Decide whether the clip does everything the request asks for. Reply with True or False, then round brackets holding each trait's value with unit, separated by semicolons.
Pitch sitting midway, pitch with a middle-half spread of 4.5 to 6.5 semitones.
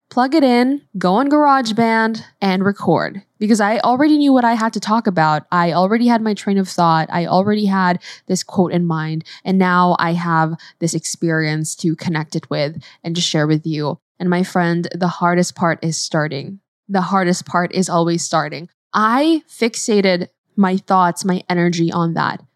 False (180 Hz; 3.8 semitones)